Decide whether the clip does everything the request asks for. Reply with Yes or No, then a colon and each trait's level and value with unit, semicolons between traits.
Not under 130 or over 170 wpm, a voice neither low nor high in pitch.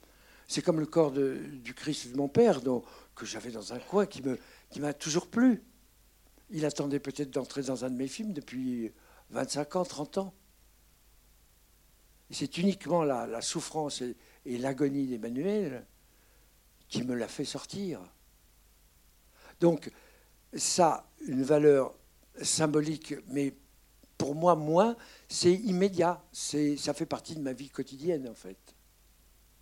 Yes: slow, 145 wpm; medium, 145 Hz